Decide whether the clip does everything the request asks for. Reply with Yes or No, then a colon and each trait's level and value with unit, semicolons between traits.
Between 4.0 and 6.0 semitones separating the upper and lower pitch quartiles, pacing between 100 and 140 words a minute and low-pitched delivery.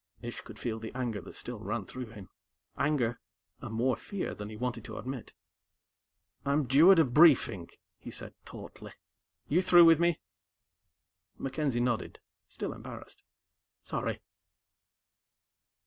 Yes: average, 5.1 semitones; slow, 135 wpm; low, 125 Hz